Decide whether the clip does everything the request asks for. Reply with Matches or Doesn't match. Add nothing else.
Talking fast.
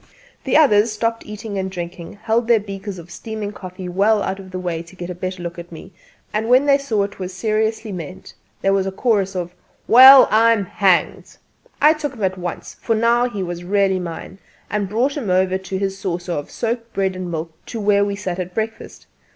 Matches